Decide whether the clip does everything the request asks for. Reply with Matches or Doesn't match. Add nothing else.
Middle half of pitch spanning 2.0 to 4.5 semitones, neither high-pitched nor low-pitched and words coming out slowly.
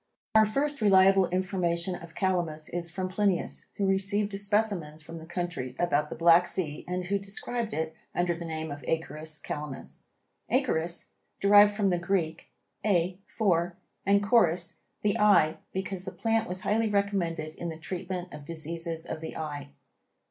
Doesn't match